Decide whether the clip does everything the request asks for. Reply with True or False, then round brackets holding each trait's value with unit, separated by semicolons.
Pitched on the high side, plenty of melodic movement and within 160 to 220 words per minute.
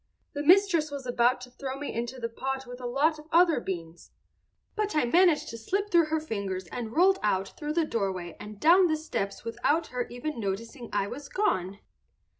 True (255 Hz; 5.9 semitones; 200 wpm)